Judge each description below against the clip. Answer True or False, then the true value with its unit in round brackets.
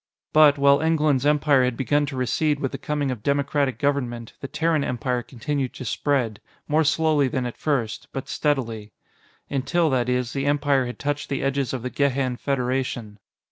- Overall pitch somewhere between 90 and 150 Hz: True (140 Hz)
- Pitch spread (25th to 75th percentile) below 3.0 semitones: True (2.6 semitones)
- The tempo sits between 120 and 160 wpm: False (180 wpm)